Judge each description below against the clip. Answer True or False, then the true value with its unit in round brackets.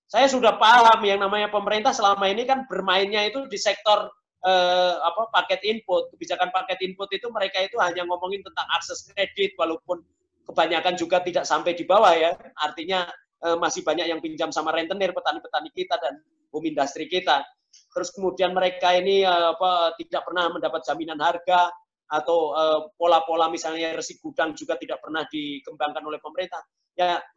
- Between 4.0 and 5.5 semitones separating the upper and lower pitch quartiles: False (3.6 semitones)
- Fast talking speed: True (160 wpm)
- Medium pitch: True (180 Hz)